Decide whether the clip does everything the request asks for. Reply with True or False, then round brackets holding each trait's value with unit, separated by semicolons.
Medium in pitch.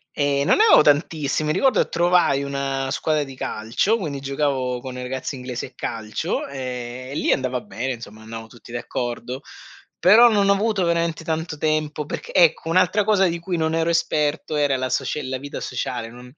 True (145 Hz)